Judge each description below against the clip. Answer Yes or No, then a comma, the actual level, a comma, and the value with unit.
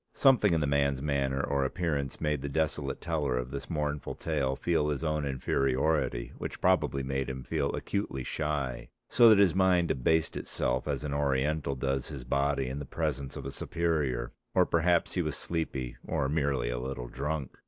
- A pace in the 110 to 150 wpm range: No, average, 185 wpm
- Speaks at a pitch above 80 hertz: No, very low, 70 Hz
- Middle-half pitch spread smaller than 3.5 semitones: Yes, average, 2.9 semitones